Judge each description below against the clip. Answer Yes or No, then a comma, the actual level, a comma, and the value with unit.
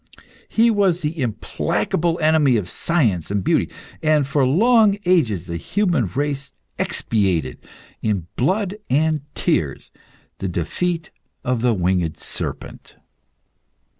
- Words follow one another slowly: Yes, slow, 115 wpm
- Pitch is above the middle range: No, medium, 140 Hz